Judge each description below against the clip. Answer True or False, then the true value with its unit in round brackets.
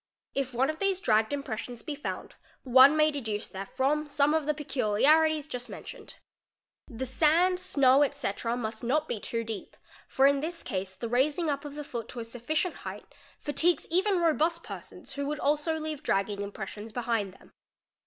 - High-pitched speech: True (280 Hz)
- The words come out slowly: False (175 wpm)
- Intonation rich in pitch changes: False (5.0 semitones)